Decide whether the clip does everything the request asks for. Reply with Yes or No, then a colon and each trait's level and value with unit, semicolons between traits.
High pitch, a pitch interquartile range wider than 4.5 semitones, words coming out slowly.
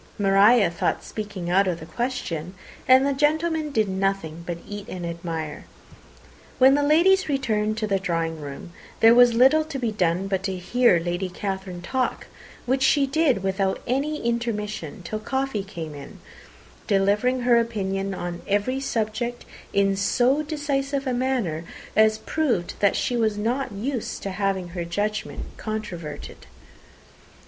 No: high, 210 Hz; wide, 5.4 semitones; average, 150 wpm